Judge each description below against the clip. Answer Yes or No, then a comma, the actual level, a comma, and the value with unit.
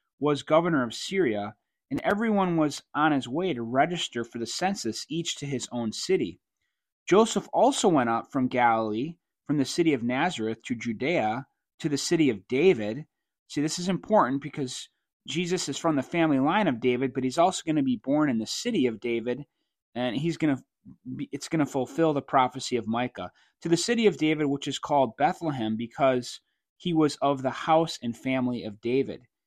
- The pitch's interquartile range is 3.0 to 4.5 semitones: No, wide, 5.4 semitones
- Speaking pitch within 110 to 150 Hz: Yes, medium, 140 Hz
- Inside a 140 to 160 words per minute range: No, average, 195 wpm